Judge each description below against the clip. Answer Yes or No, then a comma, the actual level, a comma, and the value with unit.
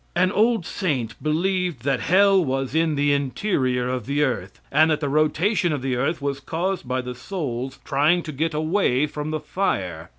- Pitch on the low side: No, medium, 150 Hz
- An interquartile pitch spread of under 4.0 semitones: No, average, 5.0 semitones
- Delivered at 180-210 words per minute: Yes, average, 190 wpm